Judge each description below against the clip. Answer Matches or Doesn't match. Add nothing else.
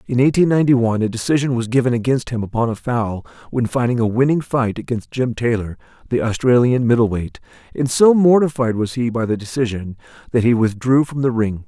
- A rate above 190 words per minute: Matches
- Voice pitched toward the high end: Doesn't match